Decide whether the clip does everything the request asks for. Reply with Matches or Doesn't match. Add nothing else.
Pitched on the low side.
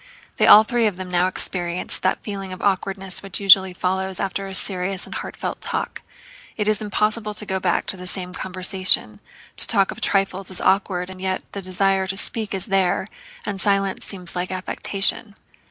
Doesn't match